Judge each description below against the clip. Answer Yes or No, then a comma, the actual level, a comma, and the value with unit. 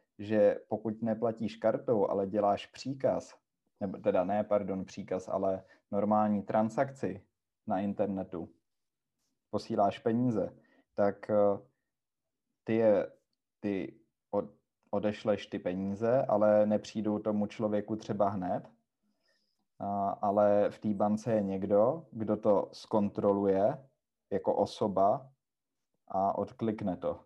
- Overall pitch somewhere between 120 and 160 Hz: No, low, 105 Hz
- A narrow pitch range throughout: Yes, narrow, 1.4 semitones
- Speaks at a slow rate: Yes, slow, 105 wpm